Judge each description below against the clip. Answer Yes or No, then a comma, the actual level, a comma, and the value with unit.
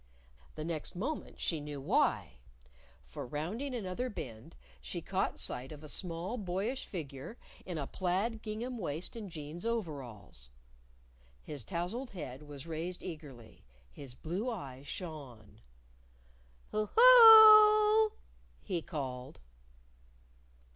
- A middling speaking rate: No, slow, 120 wpm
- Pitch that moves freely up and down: Yes, wide, 8.1 semitones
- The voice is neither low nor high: Yes, medium, 170 Hz